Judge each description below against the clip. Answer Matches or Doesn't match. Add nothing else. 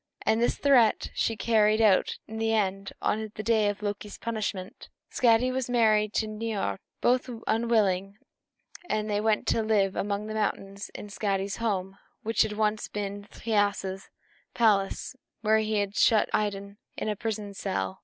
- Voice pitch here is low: Doesn't match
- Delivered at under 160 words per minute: Doesn't match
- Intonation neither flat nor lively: Doesn't match